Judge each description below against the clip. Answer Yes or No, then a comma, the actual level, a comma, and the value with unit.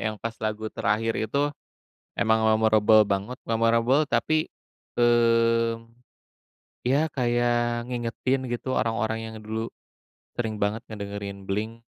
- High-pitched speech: No, low, 115 Hz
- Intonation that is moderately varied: No, narrow, 1.7 semitones